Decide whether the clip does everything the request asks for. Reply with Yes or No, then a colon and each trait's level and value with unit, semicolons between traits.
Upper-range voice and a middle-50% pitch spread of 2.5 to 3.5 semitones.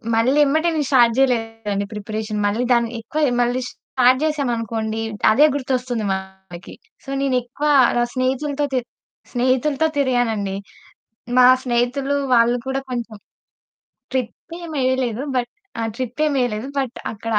Yes: high, 245 Hz; average, 3.1 semitones